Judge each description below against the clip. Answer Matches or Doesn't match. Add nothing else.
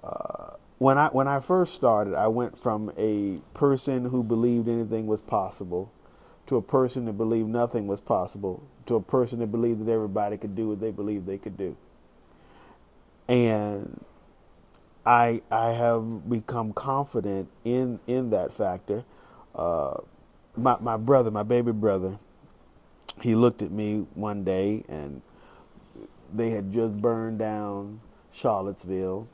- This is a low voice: Matches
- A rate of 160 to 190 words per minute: Doesn't match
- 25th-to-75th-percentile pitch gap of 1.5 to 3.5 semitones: Matches